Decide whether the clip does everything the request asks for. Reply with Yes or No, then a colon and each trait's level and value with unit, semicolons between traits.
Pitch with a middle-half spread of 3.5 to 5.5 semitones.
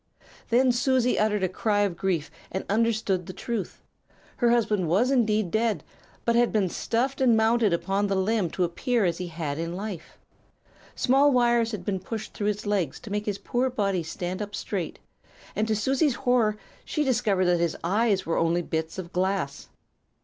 Yes: average, 4.3 semitones